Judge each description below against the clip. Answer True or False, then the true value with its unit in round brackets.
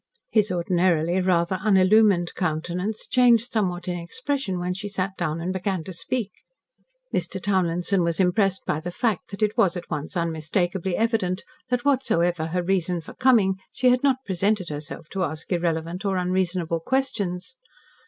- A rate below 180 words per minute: True (160 wpm)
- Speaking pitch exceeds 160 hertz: True (185 Hz)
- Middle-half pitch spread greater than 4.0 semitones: False (3.3 semitones)